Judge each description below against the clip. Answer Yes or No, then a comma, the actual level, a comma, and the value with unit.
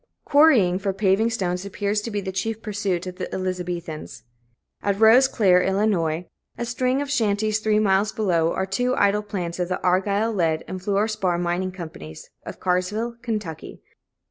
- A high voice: Yes, high, 200 Hz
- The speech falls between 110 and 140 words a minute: No, average, 165 wpm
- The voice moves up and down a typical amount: Yes, average, 3.1 semitones